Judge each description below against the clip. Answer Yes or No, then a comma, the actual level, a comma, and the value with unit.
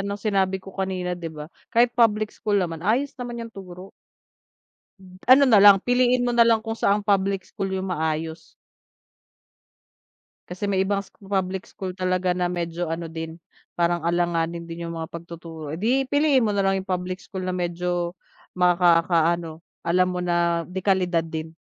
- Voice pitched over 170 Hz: Yes, medium, 185 Hz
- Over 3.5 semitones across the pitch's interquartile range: No, average, 2.8 semitones